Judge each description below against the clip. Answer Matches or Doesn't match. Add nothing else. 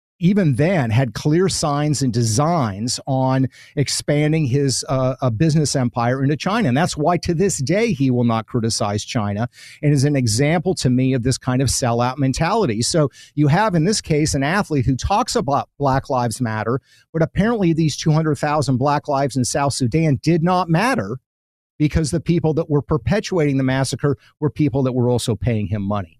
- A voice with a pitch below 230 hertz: Matches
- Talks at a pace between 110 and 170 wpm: Doesn't match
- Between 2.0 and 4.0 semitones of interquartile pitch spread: Matches